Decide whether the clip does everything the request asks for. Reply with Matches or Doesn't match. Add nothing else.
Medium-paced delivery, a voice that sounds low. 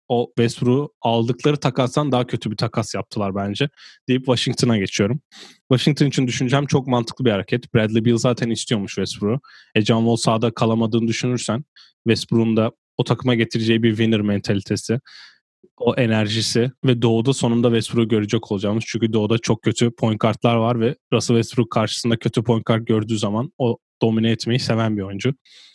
Doesn't match